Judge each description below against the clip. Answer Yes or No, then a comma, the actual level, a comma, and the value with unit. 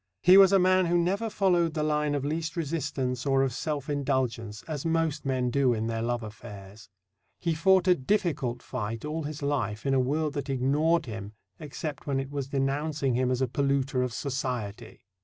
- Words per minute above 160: Yes, average, 195 wpm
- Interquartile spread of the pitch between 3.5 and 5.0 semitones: Yes, average, 3.9 semitones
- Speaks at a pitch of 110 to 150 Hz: Yes, medium, 140 Hz